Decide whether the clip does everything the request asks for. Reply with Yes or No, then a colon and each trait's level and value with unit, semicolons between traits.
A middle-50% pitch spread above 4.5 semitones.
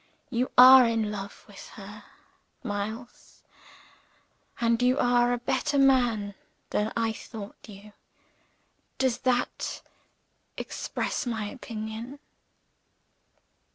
No: average, 2.8 semitones